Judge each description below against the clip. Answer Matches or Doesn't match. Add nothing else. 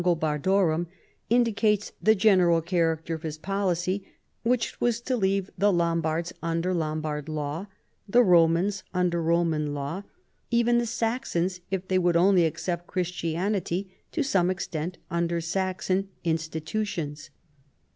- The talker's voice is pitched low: Doesn't match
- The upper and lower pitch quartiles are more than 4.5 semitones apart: Doesn't match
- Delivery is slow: Matches